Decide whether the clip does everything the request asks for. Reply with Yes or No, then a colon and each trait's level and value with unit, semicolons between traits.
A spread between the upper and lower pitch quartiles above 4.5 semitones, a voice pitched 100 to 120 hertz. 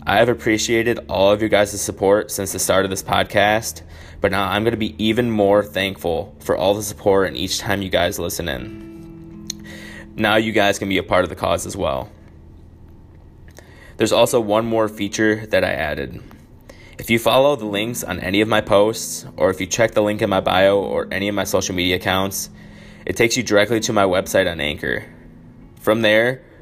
No: narrow, 2.5 semitones; low, 105 Hz